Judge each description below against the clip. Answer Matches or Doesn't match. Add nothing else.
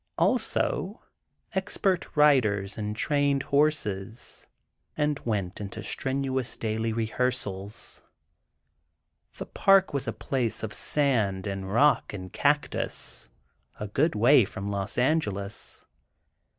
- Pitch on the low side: Matches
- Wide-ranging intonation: Matches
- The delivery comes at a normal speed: Doesn't match